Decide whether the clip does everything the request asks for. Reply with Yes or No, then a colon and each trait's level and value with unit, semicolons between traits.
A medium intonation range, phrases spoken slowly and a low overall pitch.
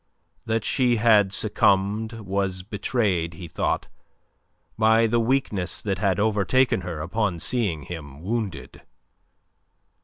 Yes: average, 3.7 semitones; slow, 115 wpm; low, 100 Hz